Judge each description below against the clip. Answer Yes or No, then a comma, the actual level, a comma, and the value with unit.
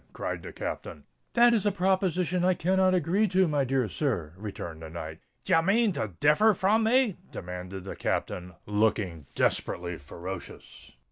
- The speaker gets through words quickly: No, average, 160 wpm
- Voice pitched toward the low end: No, medium, 150 Hz